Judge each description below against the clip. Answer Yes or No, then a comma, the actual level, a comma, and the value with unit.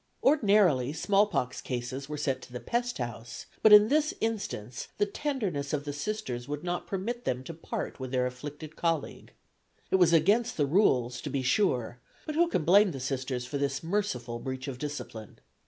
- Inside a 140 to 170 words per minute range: No, average, 190 wpm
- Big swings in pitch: Yes, wide, 8.2 semitones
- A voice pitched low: No, medium, 150 Hz